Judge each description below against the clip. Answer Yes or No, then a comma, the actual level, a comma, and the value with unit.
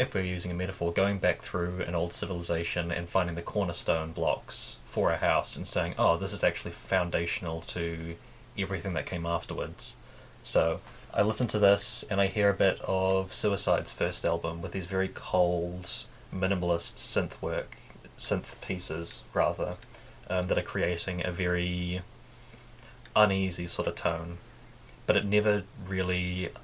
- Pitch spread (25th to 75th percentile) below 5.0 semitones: Yes, average, 3.2 semitones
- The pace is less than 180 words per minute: Yes, average, 155 wpm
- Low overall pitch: Yes, very low, 95 Hz